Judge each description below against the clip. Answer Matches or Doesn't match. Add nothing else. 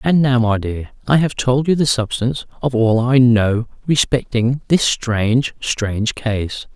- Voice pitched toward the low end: Matches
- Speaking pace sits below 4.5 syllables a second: Matches